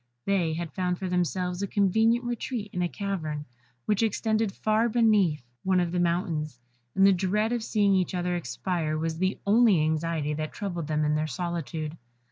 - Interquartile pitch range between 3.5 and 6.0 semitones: Yes, average, 4.1 semitones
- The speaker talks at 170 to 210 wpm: Yes, average, 180 wpm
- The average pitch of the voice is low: No, medium, 180 Hz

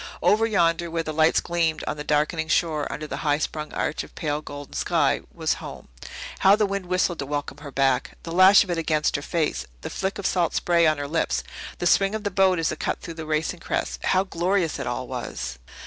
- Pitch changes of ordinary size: Yes, average, 3.3 semitones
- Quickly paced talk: Yes, fast, 230 wpm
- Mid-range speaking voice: Yes, medium, 165 Hz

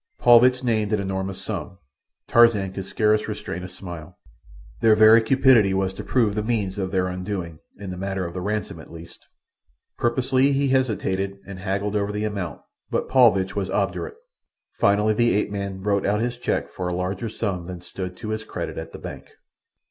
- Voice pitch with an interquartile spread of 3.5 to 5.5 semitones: No, average, 2.7 semitones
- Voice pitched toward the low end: Yes, low, 100 Hz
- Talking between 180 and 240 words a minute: Yes, average, 185 wpm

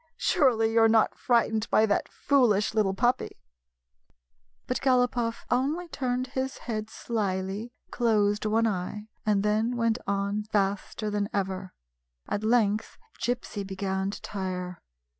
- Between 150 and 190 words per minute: No, slow, 135 wpm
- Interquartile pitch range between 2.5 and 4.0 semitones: Yes, average, 3.2 semitones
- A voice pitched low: No, high, 215 Hz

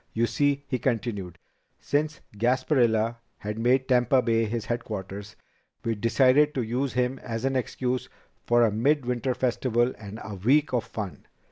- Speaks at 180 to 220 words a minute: No, average, 155 wpm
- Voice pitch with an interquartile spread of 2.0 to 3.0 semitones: Yes, narrow, 2.6 semitones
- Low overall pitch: Yes, low, 120 Hz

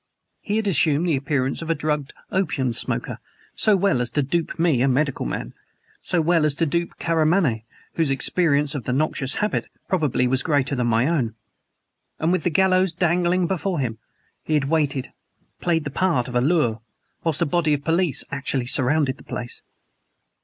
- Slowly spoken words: No, average, 180 wpm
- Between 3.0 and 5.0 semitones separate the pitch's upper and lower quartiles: Yes, average, 4.5 semitones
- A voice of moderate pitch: Yes, medium, 150 Hz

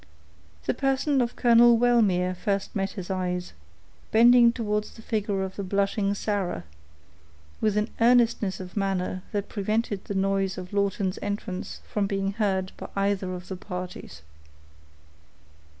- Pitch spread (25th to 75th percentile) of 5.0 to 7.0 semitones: No, average, 2.7 semitones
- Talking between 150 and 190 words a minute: No, average, 140 wpm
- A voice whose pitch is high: Yes, high, 200 Hz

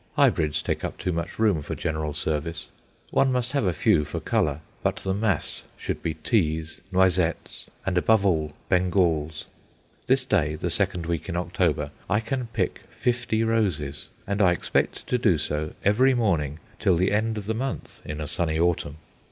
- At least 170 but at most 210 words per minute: Yes, average, 175 wpm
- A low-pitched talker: Yes, very low, 90 Hz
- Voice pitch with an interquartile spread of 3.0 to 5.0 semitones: No, wide, 5.6 semitones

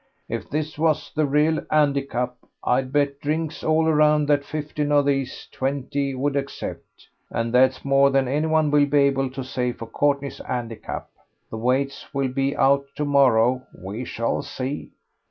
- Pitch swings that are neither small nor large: No, narrow, 2.2 semitones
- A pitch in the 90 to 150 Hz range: Yes, medium, 140 Hz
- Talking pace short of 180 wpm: Yes, average, 160 wpm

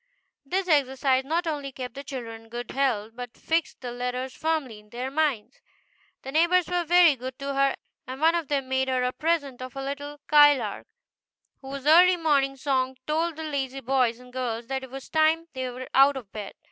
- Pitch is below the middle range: No, very high, 270 Hz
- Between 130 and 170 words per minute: No, average, 200 wpm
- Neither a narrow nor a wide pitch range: Yes, average, 3.3 semitones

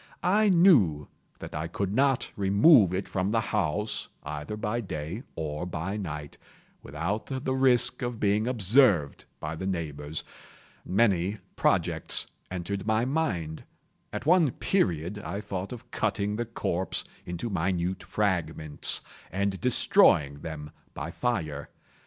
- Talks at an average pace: No, slow, 130 wpm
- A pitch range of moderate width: No, wide, 6.0 semitones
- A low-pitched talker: Yes, very low, 95 Hz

